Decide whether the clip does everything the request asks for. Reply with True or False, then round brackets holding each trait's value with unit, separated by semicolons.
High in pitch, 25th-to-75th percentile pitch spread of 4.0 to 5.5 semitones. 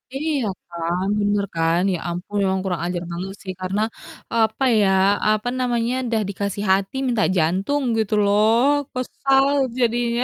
True (210 Hz; 4.5 semitones)